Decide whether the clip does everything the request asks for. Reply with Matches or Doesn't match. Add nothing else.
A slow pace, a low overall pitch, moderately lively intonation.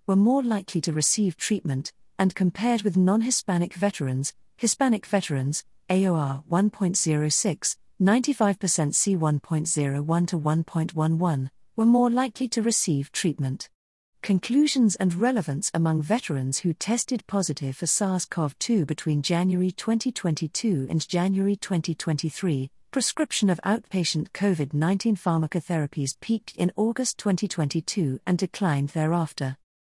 Doesn't match